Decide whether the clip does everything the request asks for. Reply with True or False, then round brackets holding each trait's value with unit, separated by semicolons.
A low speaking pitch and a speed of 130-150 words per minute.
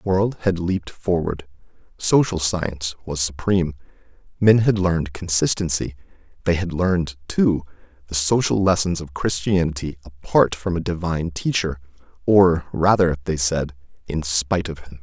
True (85 Hz; 140 wpm)